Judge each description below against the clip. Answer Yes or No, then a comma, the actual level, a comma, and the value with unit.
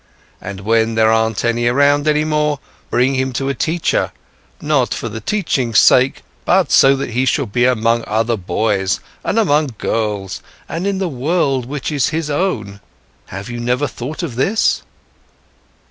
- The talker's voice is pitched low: Yes, low, 125 Hz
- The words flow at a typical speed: Yes, average, 165 wpm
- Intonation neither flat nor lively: Yes, average, 4.8 semitones